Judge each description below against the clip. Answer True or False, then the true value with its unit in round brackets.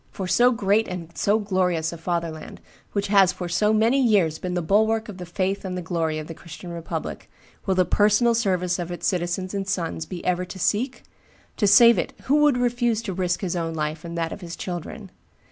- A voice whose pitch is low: False (185 Hz)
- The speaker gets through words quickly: True (220 wpm)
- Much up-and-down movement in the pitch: False (3.6 semitones)